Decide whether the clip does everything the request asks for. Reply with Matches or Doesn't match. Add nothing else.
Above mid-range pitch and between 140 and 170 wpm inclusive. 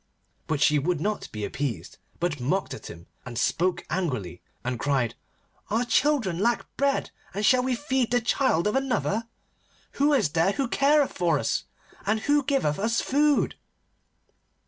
Matches